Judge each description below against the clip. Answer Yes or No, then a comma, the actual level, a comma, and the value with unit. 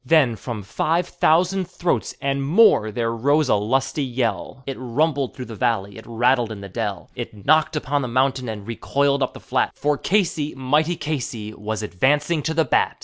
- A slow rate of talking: No, average, 190 wpm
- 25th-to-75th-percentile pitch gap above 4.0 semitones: Yes, average, 4.9 semitones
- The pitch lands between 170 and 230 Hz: No, low, 135 Hz